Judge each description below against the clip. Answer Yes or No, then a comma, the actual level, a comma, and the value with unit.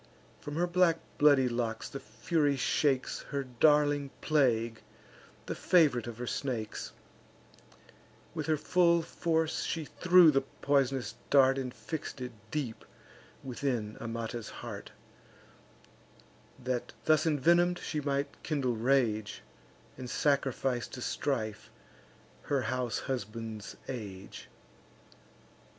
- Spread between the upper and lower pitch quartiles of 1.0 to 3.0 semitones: No, average, 4.1 semitones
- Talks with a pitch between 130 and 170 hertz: Yes, low, 135 Hz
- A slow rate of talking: Yes, slow, 110 wpm